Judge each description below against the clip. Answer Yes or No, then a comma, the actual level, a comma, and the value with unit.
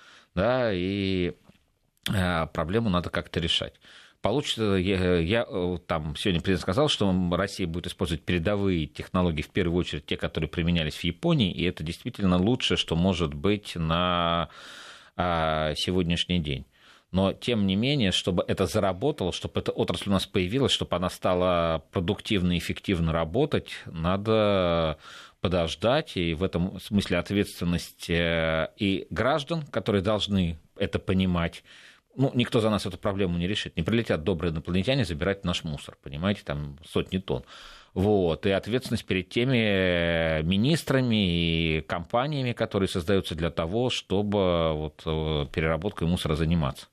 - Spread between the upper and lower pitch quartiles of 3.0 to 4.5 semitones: Yes, average, 3.3 semitones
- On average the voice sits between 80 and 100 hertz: Yes, very low, 90 Hz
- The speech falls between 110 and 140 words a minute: Yes, average, 135 wpm